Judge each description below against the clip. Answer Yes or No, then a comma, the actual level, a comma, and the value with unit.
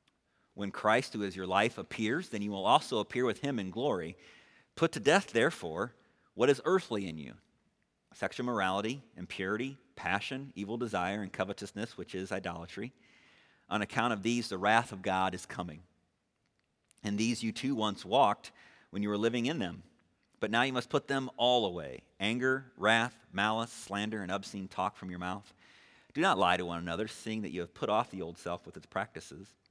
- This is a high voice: No, low, 105 Hz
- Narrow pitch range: No, average, 3.8 semitones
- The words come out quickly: No, average, 190 wpm